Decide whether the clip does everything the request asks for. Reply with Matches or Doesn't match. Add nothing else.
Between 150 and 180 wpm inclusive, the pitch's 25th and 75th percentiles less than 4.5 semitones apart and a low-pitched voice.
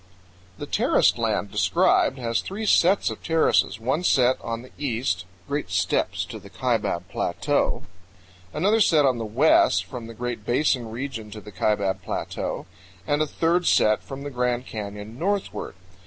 Doesn't match